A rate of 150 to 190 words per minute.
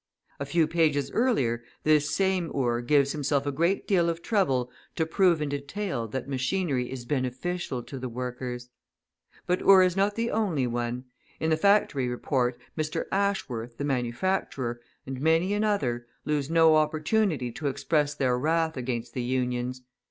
Yes: average, 160 wpm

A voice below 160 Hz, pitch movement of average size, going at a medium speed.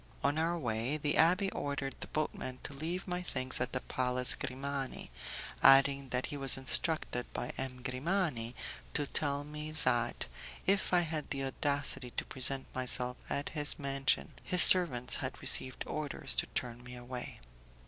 Yes: medium, 140 Hz; average, 3.2 semitones; average, 160 wpm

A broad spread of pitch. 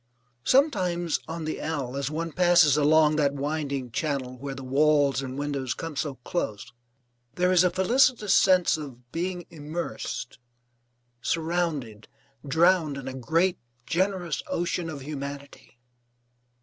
No: average, 4.0 semitones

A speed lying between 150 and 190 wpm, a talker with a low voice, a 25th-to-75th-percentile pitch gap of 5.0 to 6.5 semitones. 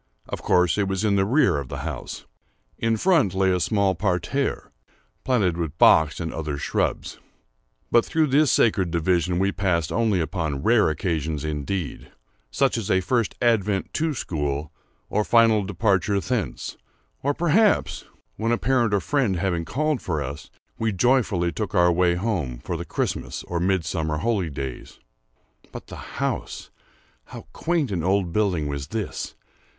Yes: average, 155 wpm; very low, 95 Hz; wide, 5.4 semitones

